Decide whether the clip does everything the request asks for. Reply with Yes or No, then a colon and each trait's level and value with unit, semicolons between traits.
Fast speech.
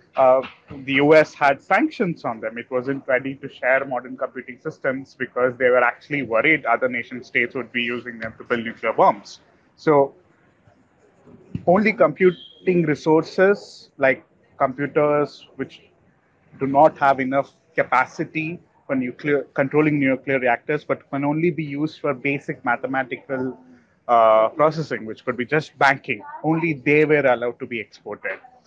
Yes: fast, 145 wpm